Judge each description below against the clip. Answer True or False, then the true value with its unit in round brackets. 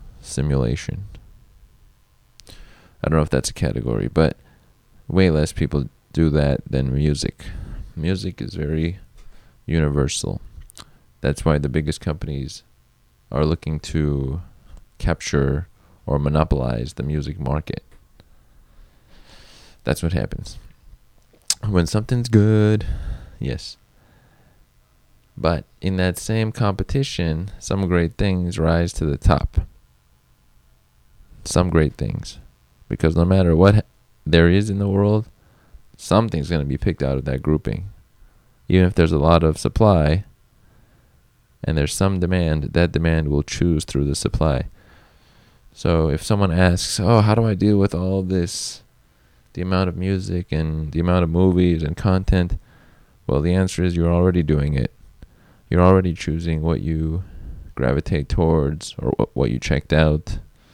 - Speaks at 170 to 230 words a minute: False (135 wpm)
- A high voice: False (80 Hz)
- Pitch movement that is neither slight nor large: True (4.3 semitones)